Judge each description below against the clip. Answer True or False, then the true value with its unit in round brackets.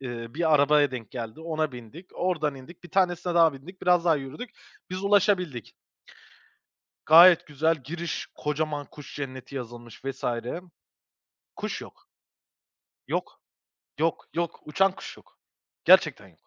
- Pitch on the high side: False (155 Hz)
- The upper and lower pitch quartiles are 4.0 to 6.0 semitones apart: True (4.3 semitones)